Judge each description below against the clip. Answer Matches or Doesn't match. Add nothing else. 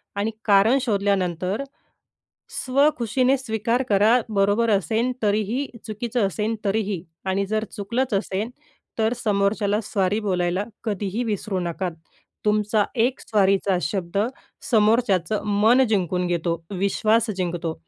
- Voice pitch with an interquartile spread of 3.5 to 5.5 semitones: Doesn't match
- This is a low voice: Doesn't match